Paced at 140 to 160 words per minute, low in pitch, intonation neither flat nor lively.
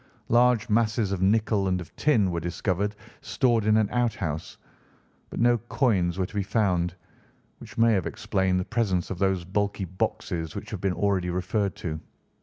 No: average, 180 wpm; low, 100 Hz; average, 3.4 semitones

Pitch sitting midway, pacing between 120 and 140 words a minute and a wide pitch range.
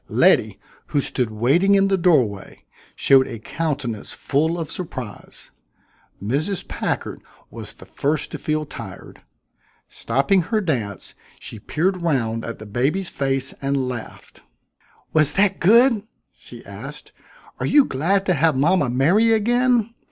Yes: medium, 155 Hz; slow, 135 wpm; wide, 7.0 semitones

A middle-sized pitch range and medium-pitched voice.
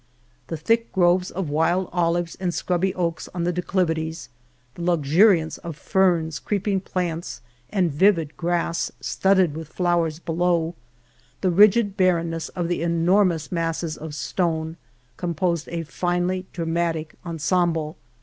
No: narrow, 2.0 semitones; medium, 170 Hz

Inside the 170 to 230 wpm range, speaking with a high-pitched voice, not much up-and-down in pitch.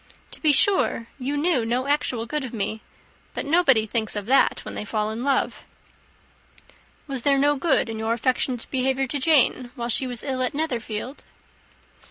No: average, 180 wpm; very high, 255 Hz; average, 3.7 semitones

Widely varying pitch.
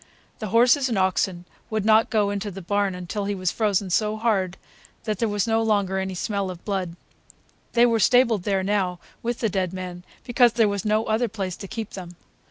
No: average, 2.9 semitones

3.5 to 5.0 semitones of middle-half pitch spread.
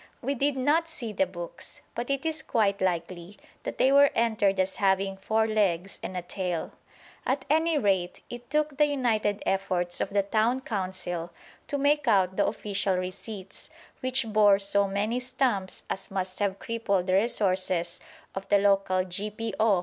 Yes: average, 4.6 semitones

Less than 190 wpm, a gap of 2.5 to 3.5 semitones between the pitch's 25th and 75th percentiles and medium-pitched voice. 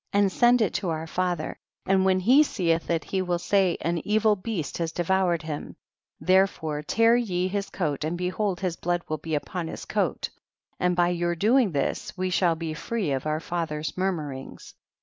No: average, 195 wpm; average, 3.1 semitones; medium, 180 Hz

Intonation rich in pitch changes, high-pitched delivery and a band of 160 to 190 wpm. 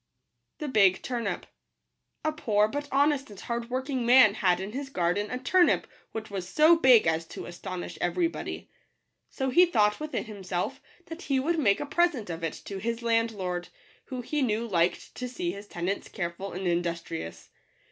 Yes: wide, 6.4 semitones; high, 220 Hz; average, 175 wpm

